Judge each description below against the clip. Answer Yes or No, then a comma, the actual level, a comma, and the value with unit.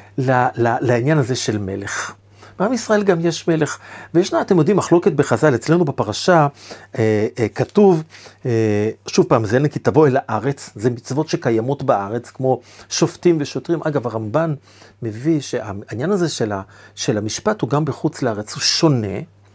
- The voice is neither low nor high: No, low, 130 Hz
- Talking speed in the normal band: No, fast, 155 wpm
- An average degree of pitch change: No, wide, 6.3 semitones